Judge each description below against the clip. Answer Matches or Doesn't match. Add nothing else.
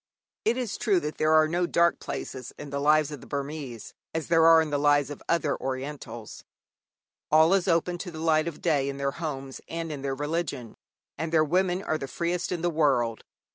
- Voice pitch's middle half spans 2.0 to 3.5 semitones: Matches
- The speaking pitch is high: Doesn't match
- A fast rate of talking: Matches